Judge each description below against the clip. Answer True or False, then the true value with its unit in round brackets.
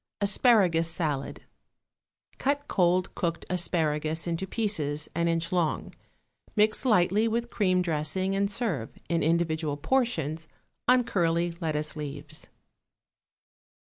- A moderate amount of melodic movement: True (4.2 semitones)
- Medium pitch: True (170 Hz)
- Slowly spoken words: True (110 wpm)